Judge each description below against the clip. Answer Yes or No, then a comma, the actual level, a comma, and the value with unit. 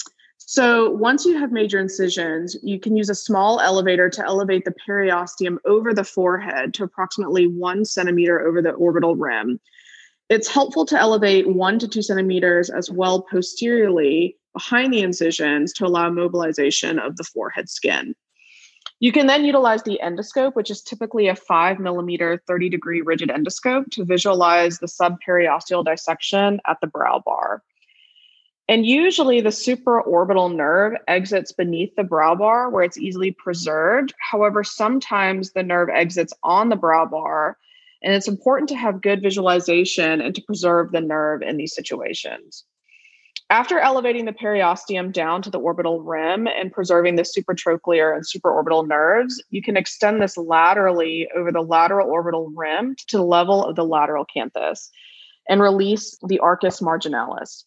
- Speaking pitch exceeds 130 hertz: Yes, high, 190 Hz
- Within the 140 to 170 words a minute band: Yes, average, 155 wpm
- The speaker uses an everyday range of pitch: Yes, average, 4.1 semitones